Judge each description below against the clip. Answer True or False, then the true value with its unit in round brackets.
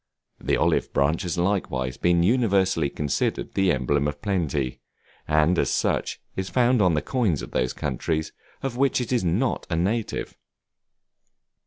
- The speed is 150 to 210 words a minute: True (155 wpm)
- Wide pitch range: True (5.9 semitones)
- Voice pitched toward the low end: True (90 Hz)